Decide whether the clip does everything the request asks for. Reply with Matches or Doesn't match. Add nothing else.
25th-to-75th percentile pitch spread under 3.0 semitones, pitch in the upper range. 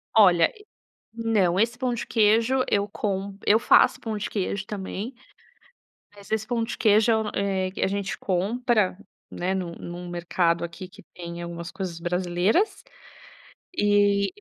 Doesn't match